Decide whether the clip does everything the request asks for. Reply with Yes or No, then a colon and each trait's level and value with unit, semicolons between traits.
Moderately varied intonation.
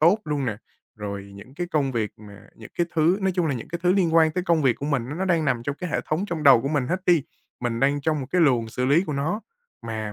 No: wide, 5.8 semitones